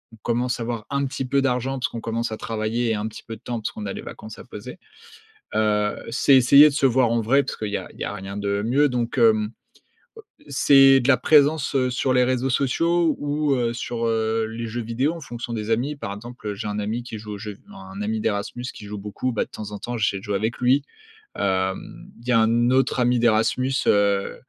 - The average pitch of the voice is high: No, low, 115 Hz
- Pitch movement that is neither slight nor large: Yes, average, 3.2 semitones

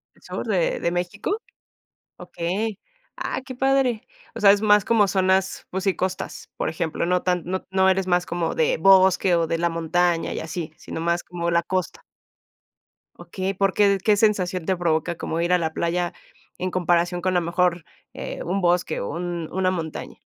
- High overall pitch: No, medium, 180 Hz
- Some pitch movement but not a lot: No, narrow, 2.2 semitones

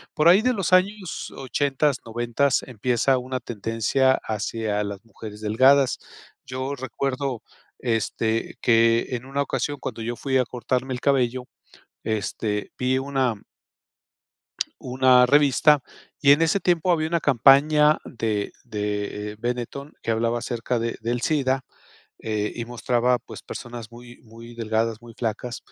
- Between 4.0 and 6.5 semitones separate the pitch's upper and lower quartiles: No, average, 3.3 semitones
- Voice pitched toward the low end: Yes, low, 125 Hz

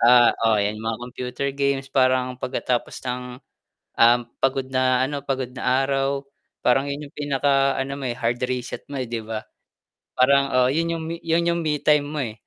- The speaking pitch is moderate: No, low, 130 Hz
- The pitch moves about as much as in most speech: No, narrow, 1.9 semitones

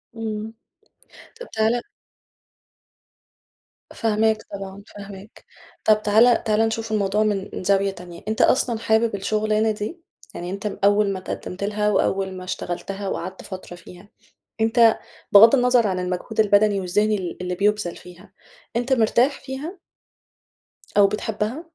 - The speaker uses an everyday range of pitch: No, narrow, 2.3 semitones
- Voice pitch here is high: Yes, high, 210 Hz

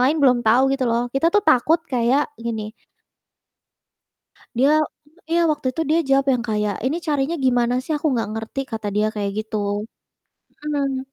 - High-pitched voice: Yes, very high, 255 Hz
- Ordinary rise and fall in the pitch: Yes, average, 4.6 semitones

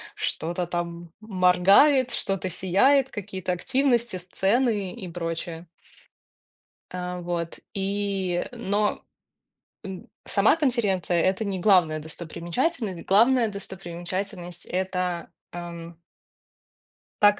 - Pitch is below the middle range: No, medium, 185 Hz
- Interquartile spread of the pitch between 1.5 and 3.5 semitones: Yes, average, 3.2 semitones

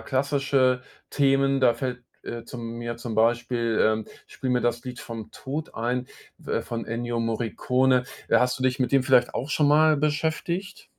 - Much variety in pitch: No, narrow, 2.6 semitones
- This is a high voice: No, low, 125 Hz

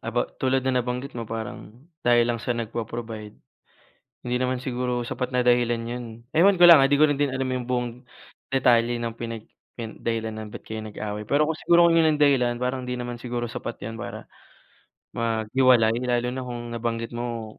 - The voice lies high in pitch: No, low, 120 Hz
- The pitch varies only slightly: Yes, narrow, 1.8 semitones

